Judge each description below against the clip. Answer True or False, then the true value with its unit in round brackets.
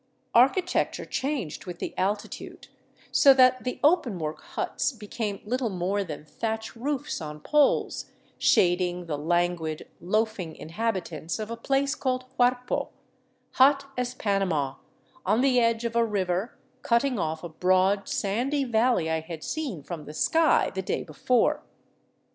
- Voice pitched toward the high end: True (210 Hz)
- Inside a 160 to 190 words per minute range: False (140 wpm)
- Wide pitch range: True (6.4 semitones)